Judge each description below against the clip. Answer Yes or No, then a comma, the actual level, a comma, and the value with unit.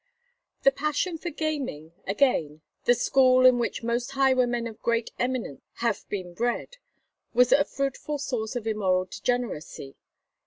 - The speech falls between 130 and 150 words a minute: Yes, average, 140 wpm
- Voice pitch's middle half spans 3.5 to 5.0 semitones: Yes, average, 3.9 semitones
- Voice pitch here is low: No, high, 245 Hz